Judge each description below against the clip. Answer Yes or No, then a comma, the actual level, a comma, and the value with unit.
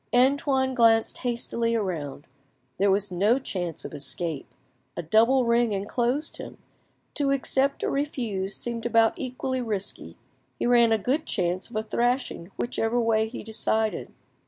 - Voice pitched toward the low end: No, high, 230 Hz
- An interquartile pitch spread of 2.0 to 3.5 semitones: No, average, 4.0 semitones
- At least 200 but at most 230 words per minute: No, average, 145 wpm